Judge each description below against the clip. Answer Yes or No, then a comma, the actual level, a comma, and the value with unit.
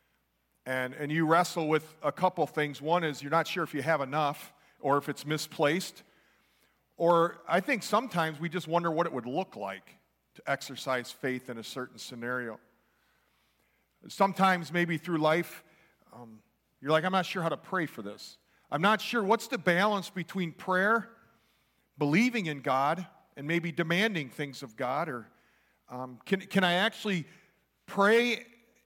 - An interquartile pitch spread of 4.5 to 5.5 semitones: Yes, average, 5.0 semitones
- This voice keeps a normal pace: Yes, average, 165 wpm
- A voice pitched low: No, medium, 165 Hz